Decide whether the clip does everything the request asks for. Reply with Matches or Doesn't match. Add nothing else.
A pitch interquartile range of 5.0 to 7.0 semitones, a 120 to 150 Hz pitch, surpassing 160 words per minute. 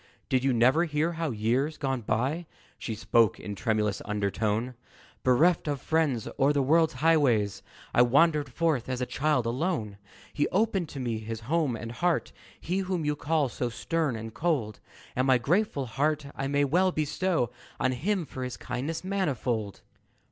Matches